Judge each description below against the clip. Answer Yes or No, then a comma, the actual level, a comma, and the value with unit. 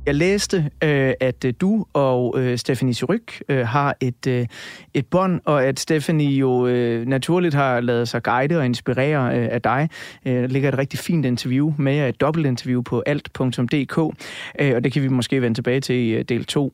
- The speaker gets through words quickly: No, average, 165 wpm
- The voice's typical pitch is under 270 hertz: Yes, low, 135 Hz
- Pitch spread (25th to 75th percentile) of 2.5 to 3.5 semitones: Yes, average, 3.0 semitones